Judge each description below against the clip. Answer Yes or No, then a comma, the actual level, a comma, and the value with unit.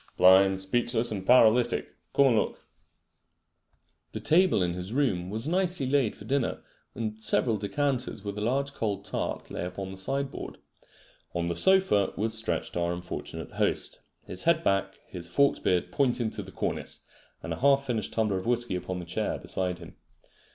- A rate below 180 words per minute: Yes, average, 170 wpm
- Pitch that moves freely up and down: Yes, wide, 5.9 semitones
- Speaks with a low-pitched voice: Yes, low, 110 Hz